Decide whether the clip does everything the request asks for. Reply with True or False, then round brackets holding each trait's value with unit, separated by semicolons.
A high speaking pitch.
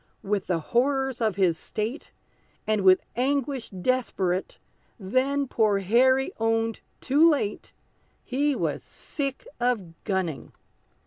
True (230 Hz)